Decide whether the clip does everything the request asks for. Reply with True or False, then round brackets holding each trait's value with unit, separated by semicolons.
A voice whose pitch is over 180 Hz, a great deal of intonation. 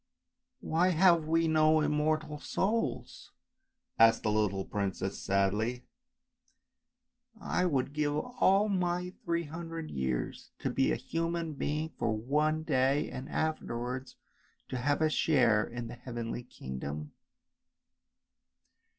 False (150 Hz; 6.0 semitones)